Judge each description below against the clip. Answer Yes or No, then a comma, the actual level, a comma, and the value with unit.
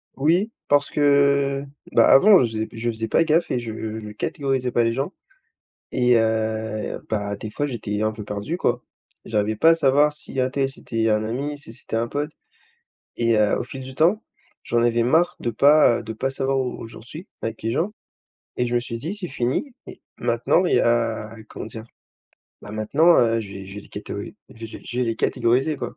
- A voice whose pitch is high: No, low, 120 Hz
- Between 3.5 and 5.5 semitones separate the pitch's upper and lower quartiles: Yes, average, 4.2 semitones